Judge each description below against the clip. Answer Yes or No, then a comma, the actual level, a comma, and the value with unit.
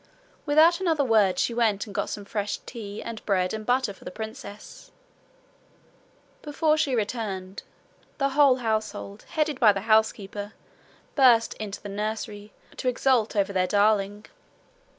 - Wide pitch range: No, average, 3.8 semitones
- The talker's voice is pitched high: Yes, high, 220 Hz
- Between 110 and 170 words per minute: Yes, average, 145 wpm